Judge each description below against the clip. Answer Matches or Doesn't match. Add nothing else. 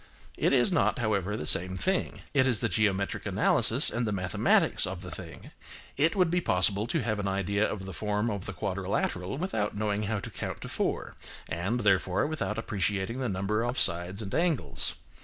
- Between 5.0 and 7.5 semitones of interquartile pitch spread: Doesn't match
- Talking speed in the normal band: Matches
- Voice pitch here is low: Matches